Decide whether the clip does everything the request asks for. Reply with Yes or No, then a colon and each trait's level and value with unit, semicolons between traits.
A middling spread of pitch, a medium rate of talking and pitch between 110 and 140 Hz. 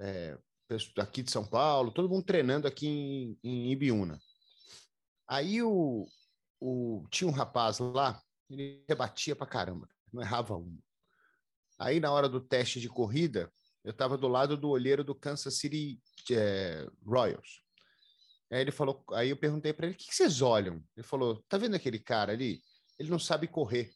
Yes: average, 4.4 semitones; average, 170 wpm; low, 135 Hz